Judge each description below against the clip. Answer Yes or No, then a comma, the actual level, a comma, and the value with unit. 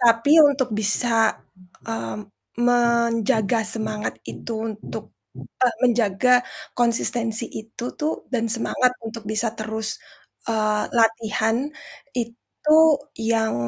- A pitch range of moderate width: No, narrow, 1.7 semitones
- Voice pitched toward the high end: Yes, high, 230 Hz